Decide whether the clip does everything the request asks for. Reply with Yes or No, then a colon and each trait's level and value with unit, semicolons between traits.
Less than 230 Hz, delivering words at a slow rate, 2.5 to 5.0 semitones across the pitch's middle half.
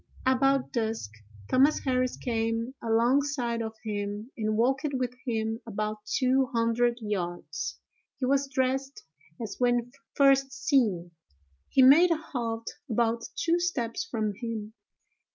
No: high, 235 Hz; slow, 125 wpm; average, 3.3 semitones